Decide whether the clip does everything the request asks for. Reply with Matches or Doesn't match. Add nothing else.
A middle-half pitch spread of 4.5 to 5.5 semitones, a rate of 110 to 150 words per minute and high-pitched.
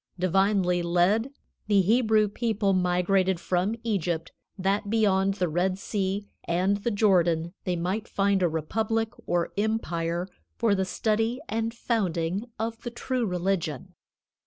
Doesn't match